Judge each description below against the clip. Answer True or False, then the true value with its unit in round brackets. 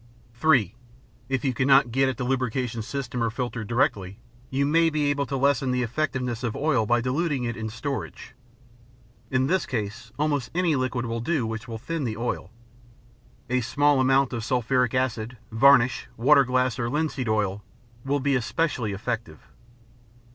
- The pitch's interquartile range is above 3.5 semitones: False (3.2 semitones)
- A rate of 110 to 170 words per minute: True (165 wpm)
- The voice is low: True (125 Hz)